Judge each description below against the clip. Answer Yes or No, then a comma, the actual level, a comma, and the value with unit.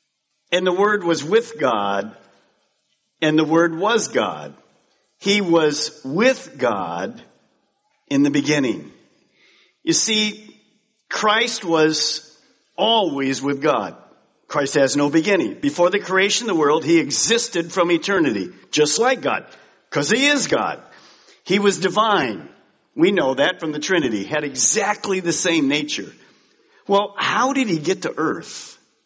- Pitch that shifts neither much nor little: No, wide, 5.7 semitones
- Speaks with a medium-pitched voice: Yes, medium, 180 Hz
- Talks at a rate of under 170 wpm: Yes, average, 140 wpm